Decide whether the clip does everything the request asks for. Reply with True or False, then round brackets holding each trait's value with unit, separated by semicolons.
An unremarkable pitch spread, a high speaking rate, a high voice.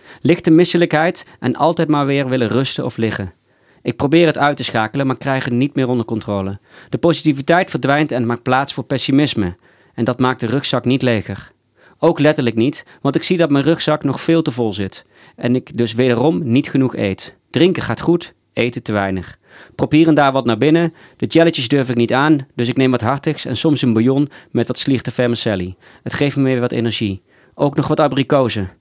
False (4.2 semitones; 205 wpm; 135 Hz)